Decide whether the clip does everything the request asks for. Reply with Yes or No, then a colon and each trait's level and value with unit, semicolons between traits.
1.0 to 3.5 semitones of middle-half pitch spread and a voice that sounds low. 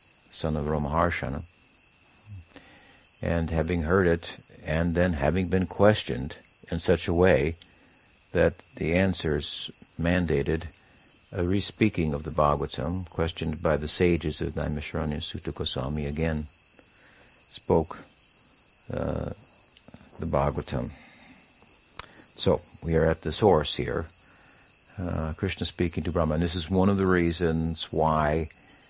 Yes: narrow, 2.6 semitones; very low, 85 Hz